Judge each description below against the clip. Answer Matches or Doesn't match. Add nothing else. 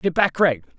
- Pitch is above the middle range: Doesn't match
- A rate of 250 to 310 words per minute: Doesn't match